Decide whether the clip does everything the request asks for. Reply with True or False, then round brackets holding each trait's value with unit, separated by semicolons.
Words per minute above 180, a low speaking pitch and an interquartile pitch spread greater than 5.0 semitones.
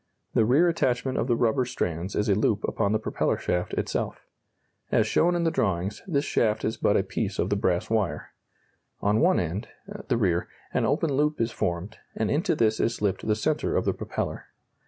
True (200 wpm; 110 Hz; 5.6 semitones)